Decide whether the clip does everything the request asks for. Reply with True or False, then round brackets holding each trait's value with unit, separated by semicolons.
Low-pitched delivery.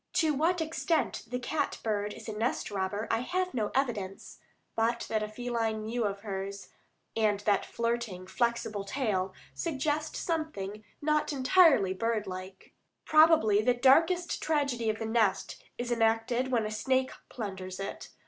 False (230 Hz)